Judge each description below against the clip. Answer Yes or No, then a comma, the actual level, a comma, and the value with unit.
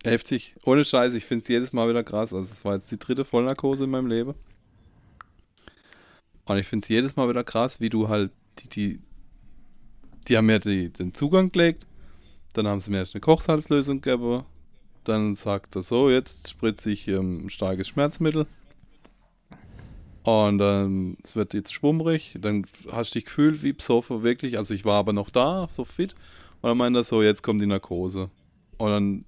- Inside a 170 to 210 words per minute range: Yes, fast, 190 wpm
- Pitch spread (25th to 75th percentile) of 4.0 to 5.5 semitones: Yes, average, 4.3 semitones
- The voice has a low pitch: Yes, low, 110 Hz